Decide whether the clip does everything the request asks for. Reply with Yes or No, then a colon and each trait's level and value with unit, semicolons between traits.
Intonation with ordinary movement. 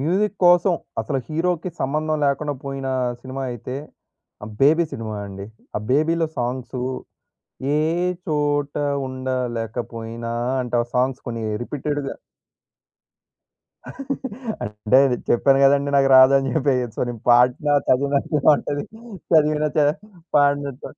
Yes: average, 3.2 semitones